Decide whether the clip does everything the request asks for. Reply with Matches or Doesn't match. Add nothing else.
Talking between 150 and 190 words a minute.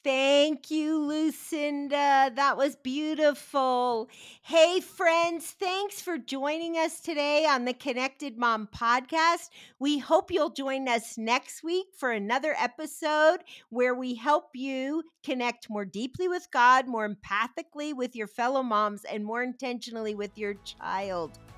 Doesn't match